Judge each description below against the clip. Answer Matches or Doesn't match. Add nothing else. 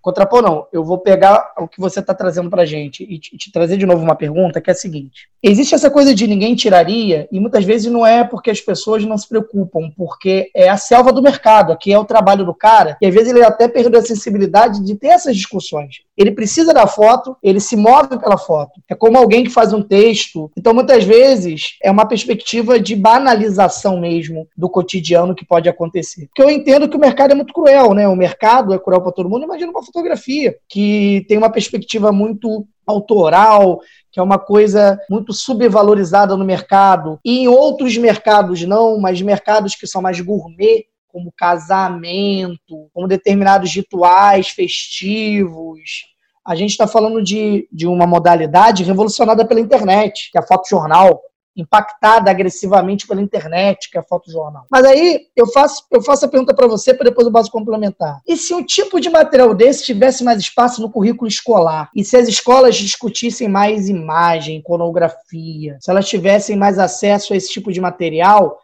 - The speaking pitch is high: Matches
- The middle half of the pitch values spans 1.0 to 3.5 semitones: Doesn't match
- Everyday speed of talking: Doesn't match